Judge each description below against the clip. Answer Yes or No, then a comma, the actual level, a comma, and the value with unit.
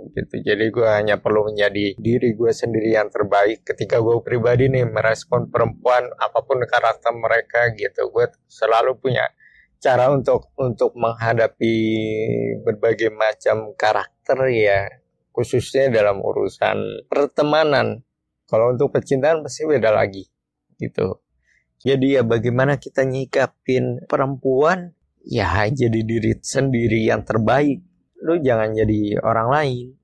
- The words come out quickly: No, average, 120 wpm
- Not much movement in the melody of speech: No, average, 3.7 semitones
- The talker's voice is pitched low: Yes, low, 120 Hz